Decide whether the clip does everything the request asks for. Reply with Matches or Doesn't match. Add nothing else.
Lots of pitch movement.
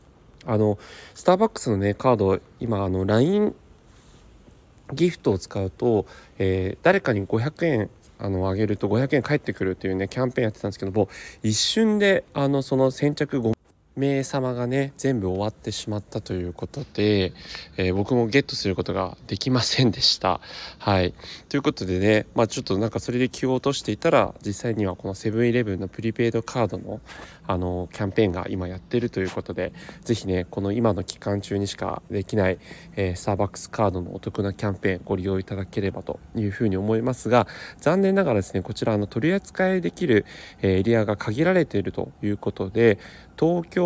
Doesn't match